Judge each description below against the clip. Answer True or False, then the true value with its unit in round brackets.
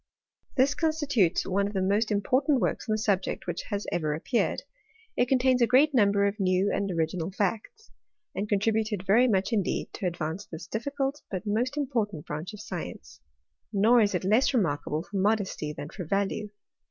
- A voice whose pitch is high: True (205 Hz)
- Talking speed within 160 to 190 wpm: True (175 wpm)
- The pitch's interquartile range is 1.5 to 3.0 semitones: False (4.2 semitones)